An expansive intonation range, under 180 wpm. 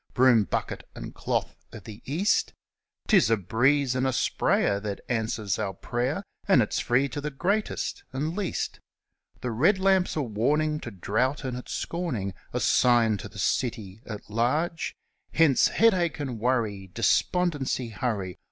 Yes: wide, 5.7 semitones; average, 155 wpm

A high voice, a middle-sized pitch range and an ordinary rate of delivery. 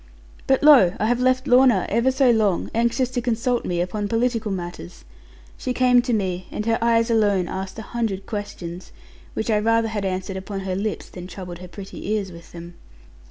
Yes: high, 215 Hz; average, 4.1 semitones; average, 195 wpm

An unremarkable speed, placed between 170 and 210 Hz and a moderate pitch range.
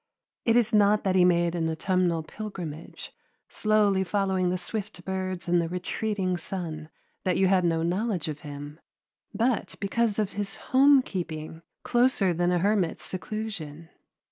Yes: average, 150 wpm; medium, 185 Hz; average, 3.5 semitones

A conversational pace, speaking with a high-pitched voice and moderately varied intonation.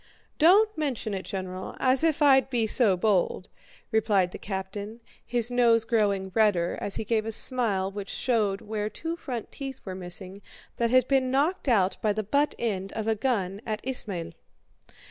Yes: average, 175 wpm; high, 220 Hz; average, 4.6 semitones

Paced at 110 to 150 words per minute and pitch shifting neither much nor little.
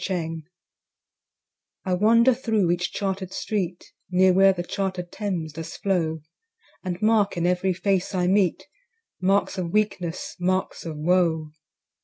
No: slow, 135 wpm; narrow, 2.2 semitones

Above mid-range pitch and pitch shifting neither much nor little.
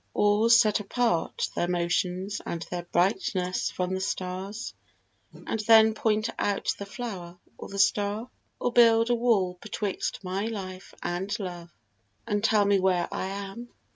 Yes: high, 200 Hz; average, 3.1 semitones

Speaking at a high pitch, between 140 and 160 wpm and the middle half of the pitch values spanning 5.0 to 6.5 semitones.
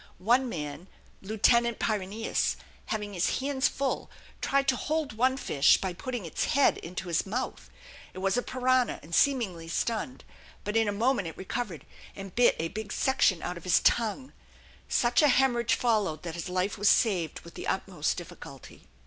No: high, 215 Hz; average, 175 wpm; wide, 5.6 semitones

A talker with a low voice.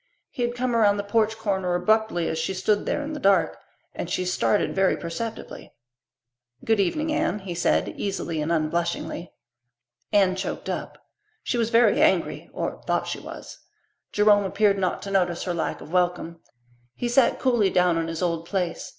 No: high, 195 Hz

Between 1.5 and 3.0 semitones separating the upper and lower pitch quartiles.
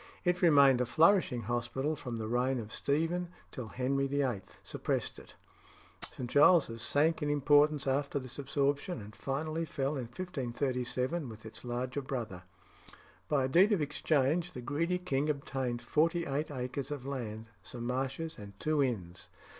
No: average, 3.7 semitones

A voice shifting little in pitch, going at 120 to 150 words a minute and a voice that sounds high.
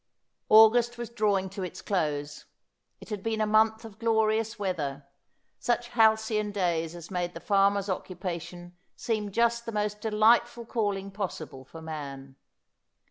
No: average, 3.9 semitones; average, 140 wpm; high, 205 Hz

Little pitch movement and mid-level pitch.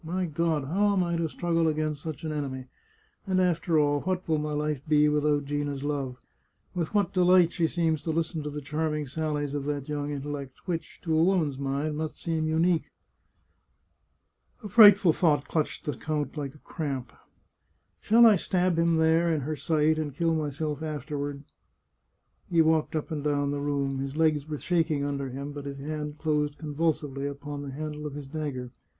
Yes: narrow, 2.2 semitones; medium, 150 Hz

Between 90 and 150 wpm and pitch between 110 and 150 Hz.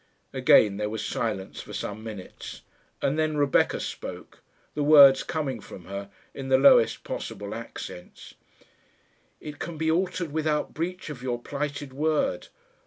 Yes: average, 145 wpm; medium, 140 Hz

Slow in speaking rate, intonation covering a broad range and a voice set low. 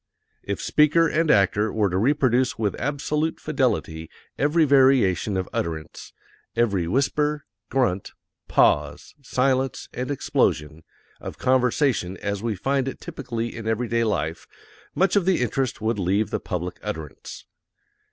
Yes: slow, 130 wpm; wide, 5.9 semitones; low, 120 Hz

